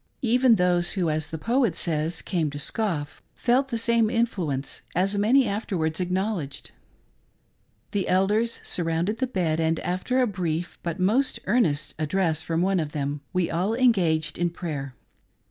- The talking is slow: No, average, 160 wpm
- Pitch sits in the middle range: Yes, medium, 180 Hz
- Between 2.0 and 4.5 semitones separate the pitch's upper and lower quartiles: No, wide, 5.5 semitones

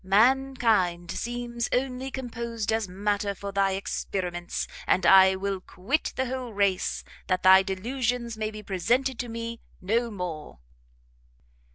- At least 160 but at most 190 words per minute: No, slow, 135 wpm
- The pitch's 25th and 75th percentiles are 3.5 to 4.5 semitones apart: Yes, average, 4.2 semitones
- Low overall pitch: No, high, 215 Hz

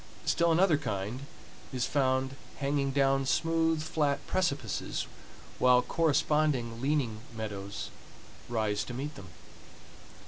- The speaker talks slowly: Yes, slow, 105 wpm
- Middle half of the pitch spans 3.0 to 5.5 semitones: Yes, average, 4.2 semitones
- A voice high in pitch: No, low, 135 Hz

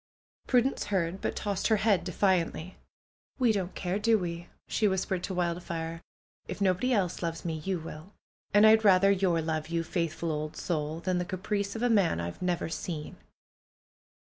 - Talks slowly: No, average, 165 wpm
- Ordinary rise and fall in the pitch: Yes, average, 3.3 semitones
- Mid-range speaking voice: Yes, medium, 180 Hz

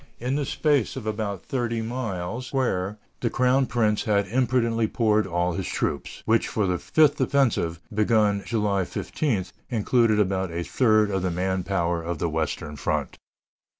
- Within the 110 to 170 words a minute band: Yes, average, 155 wpm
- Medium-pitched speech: No, low, 105 Hz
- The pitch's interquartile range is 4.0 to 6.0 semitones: Yes, average, 4.5 semitones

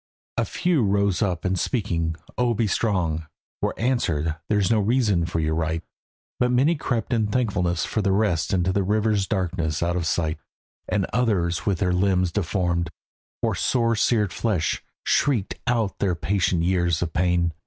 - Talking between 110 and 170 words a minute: Yes, average, 165 wpm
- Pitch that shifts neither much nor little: Yes, average, 4.1 semitones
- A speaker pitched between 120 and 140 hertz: No, very low, 95 Hz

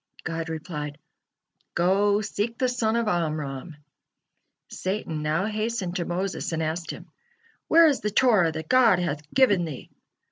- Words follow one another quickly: No, average, 145 wpm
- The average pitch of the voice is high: No, medium, 180 Hz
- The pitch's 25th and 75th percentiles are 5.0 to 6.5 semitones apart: Yes, average, 5.3 semitones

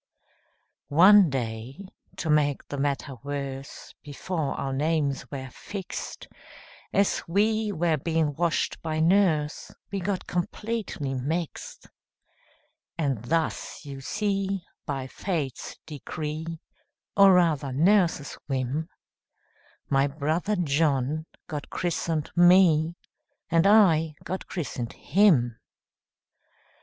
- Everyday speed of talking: No, slow, 100 wpm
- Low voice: No, medium, 155 Hz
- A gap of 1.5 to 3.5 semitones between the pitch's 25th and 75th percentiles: No, average, 4.3 semitones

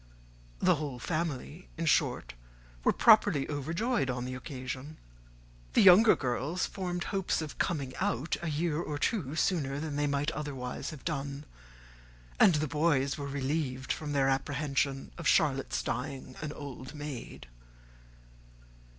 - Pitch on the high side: No, medium, 145 Hz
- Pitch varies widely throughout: No, average, 3.2 semitones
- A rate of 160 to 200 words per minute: No, average, 140 wpm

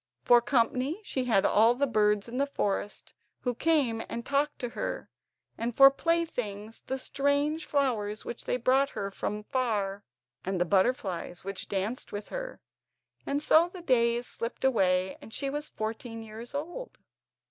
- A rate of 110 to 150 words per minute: No, average, 160 wpm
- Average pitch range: Yes, average, 5.0 semitones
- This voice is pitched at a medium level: No, high, 240 Hz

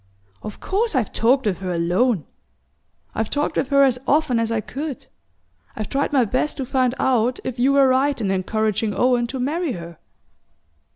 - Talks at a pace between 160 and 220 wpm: Yes, average, 180 wpm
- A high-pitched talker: Yes, very high, 250 Hz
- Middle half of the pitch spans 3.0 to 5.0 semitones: Yes, average, 4.1 semitones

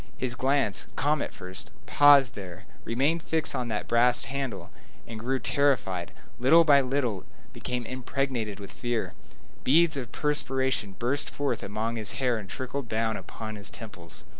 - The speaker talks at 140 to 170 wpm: Yes, average, 160 wpm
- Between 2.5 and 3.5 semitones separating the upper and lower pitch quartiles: No, average, 4.2 semitones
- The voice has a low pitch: Yes, low, 125 Hz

